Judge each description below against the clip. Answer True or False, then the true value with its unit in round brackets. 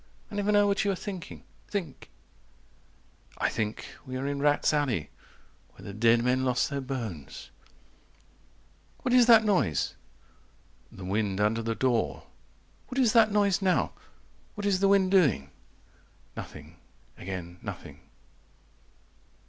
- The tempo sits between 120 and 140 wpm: True (135 wpm)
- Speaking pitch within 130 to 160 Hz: True (140 Hz)